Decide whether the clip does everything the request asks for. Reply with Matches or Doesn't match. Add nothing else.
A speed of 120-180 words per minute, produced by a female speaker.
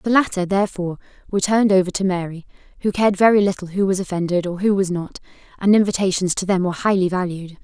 Doesn't match